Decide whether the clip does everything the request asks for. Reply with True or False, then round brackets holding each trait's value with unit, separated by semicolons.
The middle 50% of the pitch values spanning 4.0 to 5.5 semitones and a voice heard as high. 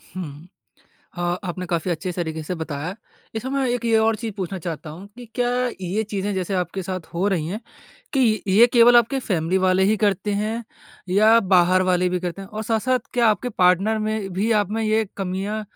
False (3.5 semitones; 195 Hz)